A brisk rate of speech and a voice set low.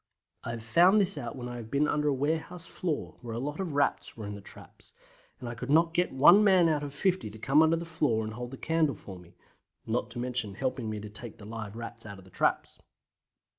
Yes: fast, 250 wpm; low, 130 Hz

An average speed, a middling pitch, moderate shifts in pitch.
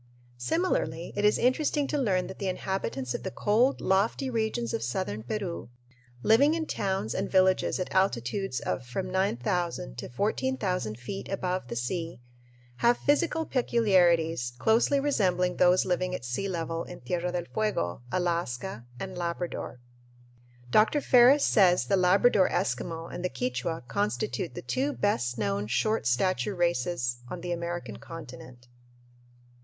No: average, 145 wpm; medium, 180 Hz; wide, 7.4 semitones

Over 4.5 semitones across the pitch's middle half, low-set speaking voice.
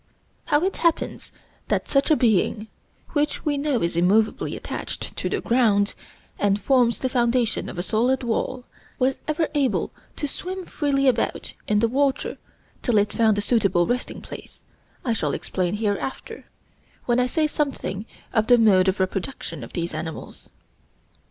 No: average, 5.1 semitones; high, 235 Hz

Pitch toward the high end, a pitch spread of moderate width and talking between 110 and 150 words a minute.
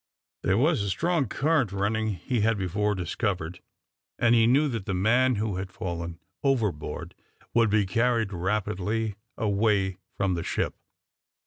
No: low, 105 Hz; average, 3.6 semitones; average, 145 wpm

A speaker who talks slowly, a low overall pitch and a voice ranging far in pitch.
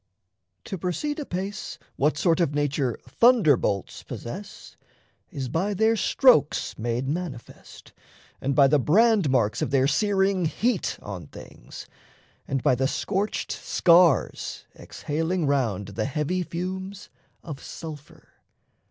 No: slow, 120 wpm; medium, 160 Hz; wide, 6.1 semitones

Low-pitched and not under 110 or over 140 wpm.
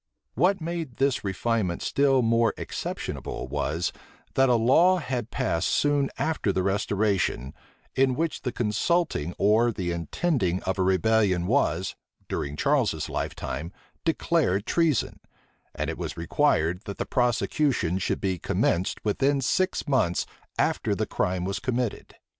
Yes: low, 110 Hz; slow, 135 wpm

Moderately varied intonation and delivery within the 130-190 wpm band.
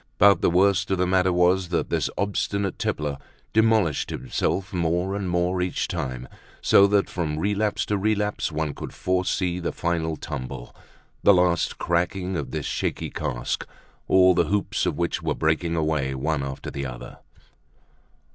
Yes: average, 3.6 semitones; average, 160 wpm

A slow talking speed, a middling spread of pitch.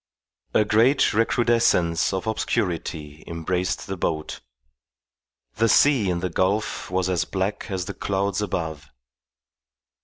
Yes: slow, 120 wpm; average, 3.9 semitones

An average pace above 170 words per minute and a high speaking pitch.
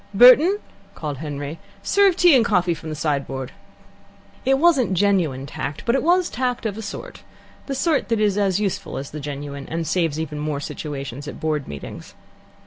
No: average, 185 wpm; medium, 170 Hz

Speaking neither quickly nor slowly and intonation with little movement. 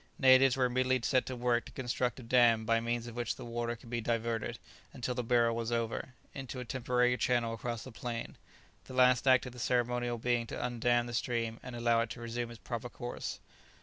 No: fast, 215 wpm; narrow, 1.2 semitones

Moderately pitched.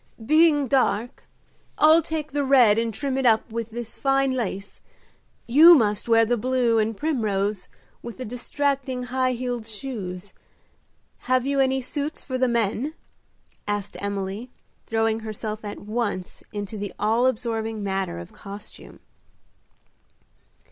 No: high, 235 Hz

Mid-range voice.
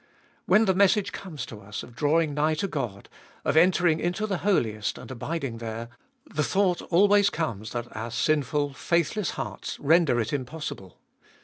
Yes: medium, 155 Hz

